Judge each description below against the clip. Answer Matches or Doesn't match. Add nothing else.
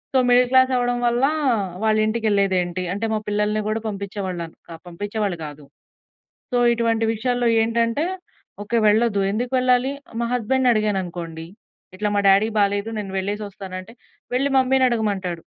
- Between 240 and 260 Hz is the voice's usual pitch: Doesn't match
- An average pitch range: Matches